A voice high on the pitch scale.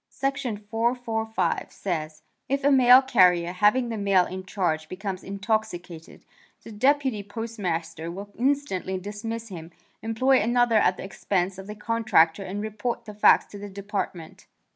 Yes: high, 205 Hz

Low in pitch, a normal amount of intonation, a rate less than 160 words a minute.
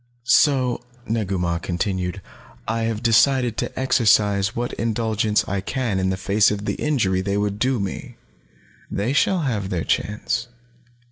Yes: low, 105 Hz; average, 3.6 semitones; average, 150 wpm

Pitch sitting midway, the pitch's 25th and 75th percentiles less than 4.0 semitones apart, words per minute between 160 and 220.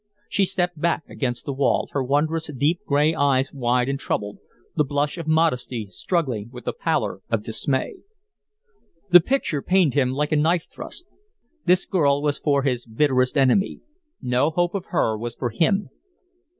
No: medium, 145 Hz; average, 4.5 semitones; average, 165 wpm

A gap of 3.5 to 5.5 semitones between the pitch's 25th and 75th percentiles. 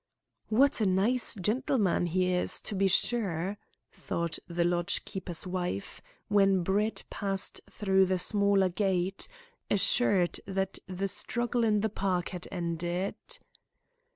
No: narrow, 2.5 semitones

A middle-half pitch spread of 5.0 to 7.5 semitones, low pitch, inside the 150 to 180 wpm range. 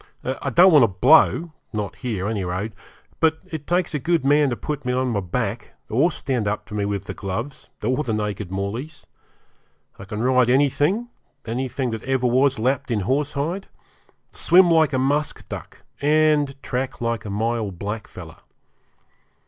Yes: wide, 5.4 semitones; low, 130 Hz; average, 170 wpm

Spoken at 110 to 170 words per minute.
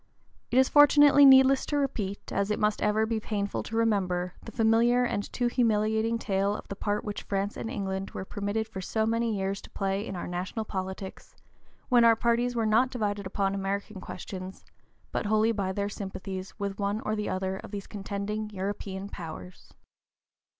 No: average, 185 wpm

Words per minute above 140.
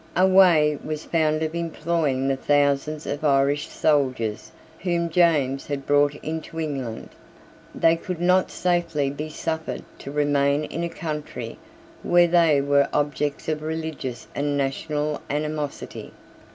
No: slow, 135 wpm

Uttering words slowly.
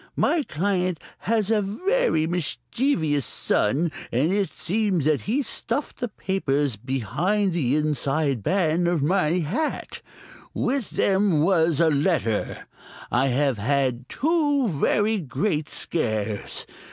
Yes: slow, 125 wpm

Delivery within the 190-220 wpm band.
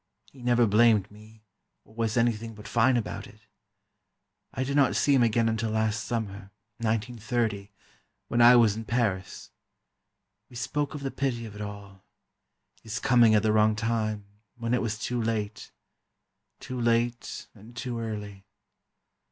No: average, 150 wpm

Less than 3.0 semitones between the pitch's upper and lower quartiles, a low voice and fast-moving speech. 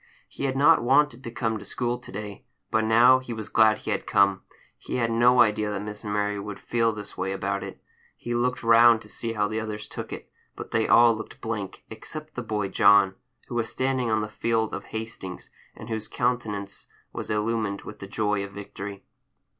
Yes: narrow, 2.5 semitones; low, 110 Hz; fast, 210 wpm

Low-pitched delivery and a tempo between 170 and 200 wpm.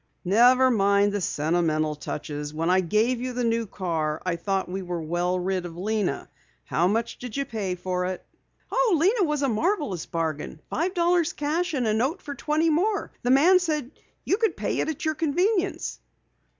No: high, 225 Hz; average, 190 wpm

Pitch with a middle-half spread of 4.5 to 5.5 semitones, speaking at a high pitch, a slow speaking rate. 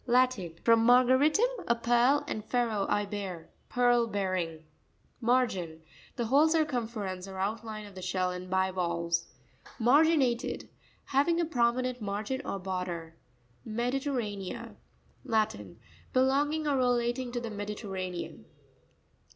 Yes: average, 5.2 semitones; high, 225 Hz; slow, 110 wpm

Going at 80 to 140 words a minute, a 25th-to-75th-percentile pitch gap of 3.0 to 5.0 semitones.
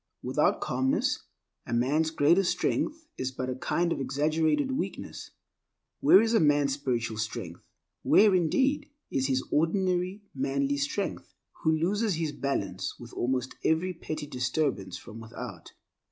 No: slow, 135 wpm; wide, 5.5 semitones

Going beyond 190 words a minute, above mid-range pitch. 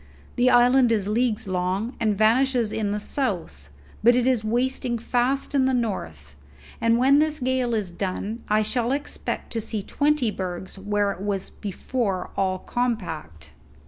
No: average, 160 wpm; high, 225 Hz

